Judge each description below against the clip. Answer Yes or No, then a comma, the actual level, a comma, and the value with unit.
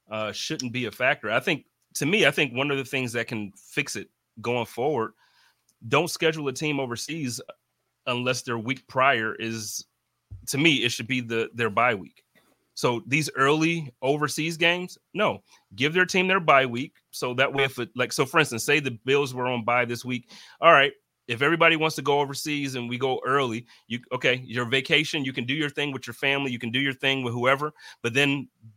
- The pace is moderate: No, fast, 215 wpm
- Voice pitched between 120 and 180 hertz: Yes, low, 135 Hz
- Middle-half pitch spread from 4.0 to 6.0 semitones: No, average, 3.5 semitones